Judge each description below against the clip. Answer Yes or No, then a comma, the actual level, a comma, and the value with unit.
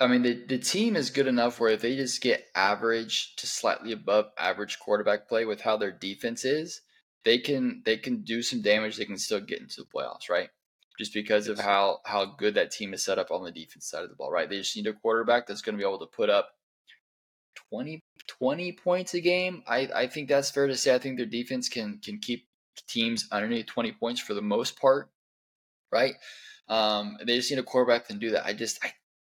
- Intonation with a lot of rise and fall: No, average, 4.2 semitones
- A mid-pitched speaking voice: No, low, 120 Hz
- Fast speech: Yes, fast, 230 wpm